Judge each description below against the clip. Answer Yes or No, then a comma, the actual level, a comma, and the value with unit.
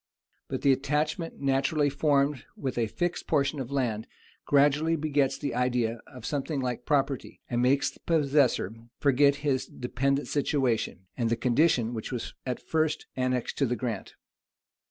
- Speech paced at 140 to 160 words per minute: Yes, average, 155 wpm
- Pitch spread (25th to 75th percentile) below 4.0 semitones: Yes, average, 2.8 semitones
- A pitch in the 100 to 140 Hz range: Yes, low, 135 Hz